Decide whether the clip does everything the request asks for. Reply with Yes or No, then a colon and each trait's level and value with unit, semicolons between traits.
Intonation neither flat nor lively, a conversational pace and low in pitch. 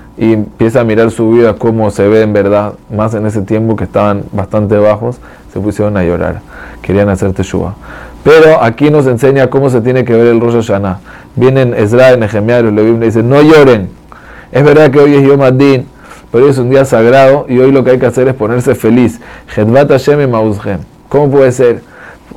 No: average, 3.7 semitones; fast, 195 wpm; low, 115 Hz